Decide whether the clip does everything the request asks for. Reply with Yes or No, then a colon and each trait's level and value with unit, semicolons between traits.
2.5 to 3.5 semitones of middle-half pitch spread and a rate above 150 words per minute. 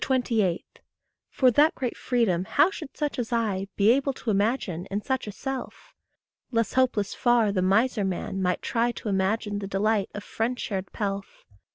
No: average, 4.1 semitones; average, 170 wpm